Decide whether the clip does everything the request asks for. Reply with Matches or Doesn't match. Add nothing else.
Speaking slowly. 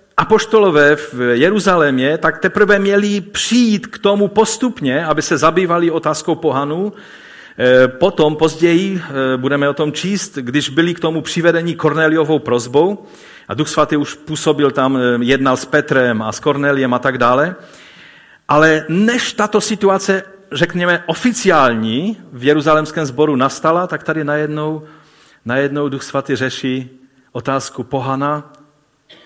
Doesn't match